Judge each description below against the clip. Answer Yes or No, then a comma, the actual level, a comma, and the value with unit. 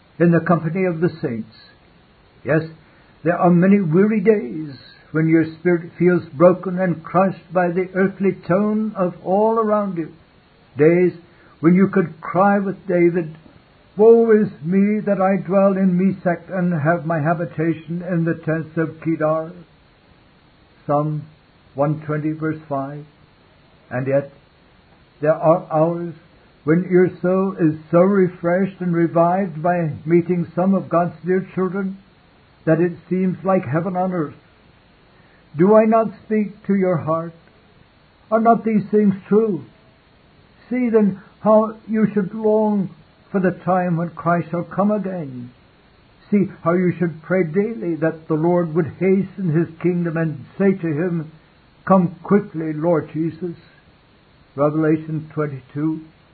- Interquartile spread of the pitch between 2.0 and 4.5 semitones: Yes, average, 2.9 semitones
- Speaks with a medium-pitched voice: Yes, medium, 175 Hz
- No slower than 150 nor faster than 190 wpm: No, average, 140 wpm